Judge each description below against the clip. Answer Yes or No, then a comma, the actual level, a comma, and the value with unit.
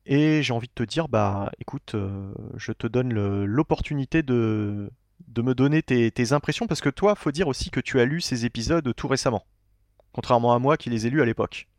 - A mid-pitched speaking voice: No, low, 120 Hz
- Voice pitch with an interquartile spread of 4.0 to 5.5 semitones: Yes, average, 4.7 semitones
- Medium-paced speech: No, fast, 225 wpm